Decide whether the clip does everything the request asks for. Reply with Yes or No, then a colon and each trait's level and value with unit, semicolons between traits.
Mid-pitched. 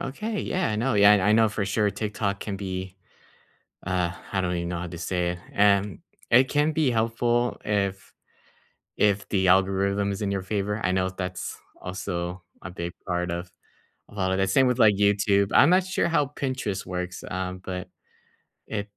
No: low, 100 Hz